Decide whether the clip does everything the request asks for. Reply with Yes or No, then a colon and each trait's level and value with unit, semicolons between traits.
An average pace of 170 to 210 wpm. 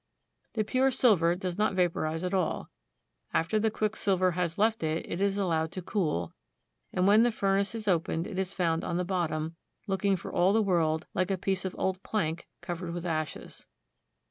Yes: average, 190 wpm